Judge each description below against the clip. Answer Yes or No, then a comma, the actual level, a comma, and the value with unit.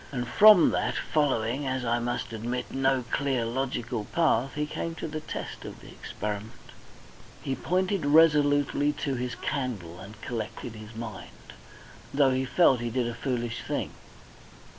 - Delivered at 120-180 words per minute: Yes, average, 150 wpm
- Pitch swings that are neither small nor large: Yes, average, 3.6 semitones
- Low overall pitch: Yes, low, 130 Hz